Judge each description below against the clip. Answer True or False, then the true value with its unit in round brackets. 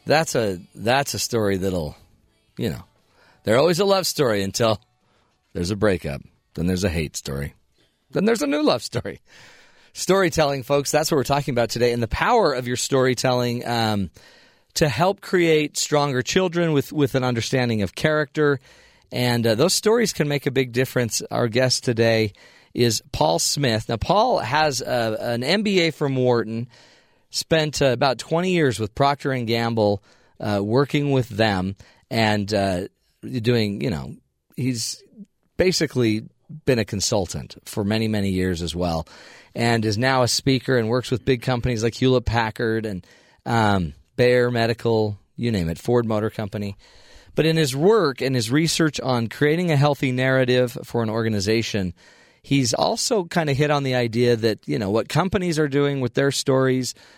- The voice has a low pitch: True (125 Hz)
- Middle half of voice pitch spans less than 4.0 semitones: False (4.7 semitones)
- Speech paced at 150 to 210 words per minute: True (165 wpm)